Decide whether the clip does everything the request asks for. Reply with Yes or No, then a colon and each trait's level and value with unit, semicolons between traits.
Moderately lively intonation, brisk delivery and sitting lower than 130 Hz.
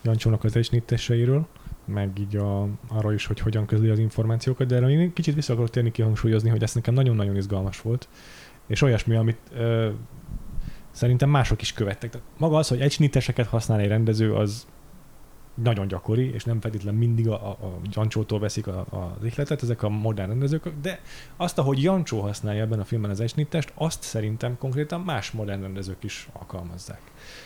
Yes: average, 3.6 semitones; fast, 175 wpm; low, 115 Hz